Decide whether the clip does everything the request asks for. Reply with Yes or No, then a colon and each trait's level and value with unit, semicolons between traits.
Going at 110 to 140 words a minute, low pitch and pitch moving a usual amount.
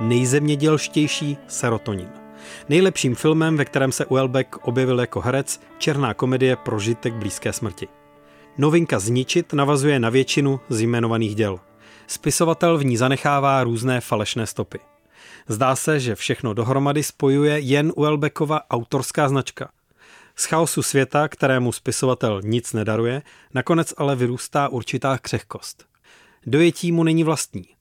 Yes: average, 120 wpm; low, 130 Hz; average, 4.2 semitones